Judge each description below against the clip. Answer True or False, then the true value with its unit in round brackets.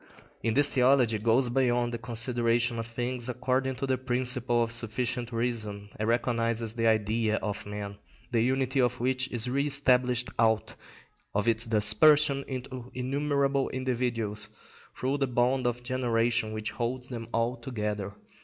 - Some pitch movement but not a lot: False (2.1 semitones)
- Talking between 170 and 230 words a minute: False (150 wpm)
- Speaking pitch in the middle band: False (120 Hz)